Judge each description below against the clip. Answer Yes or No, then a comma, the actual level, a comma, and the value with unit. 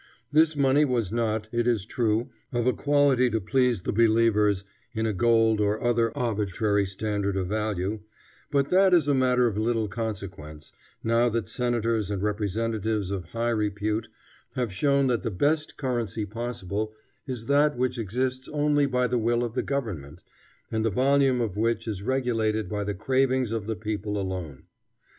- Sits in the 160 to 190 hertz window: No, low, 115 Hz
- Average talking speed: Yes, average, 170 wpm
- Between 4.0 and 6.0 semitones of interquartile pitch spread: No, average, 3.3 semitones